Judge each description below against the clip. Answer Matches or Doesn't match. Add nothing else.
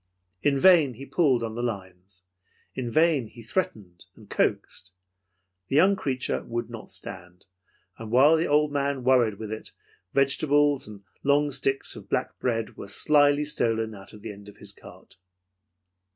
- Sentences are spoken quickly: Doesn't match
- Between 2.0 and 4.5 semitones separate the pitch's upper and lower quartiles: Doesn't match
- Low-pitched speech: Matches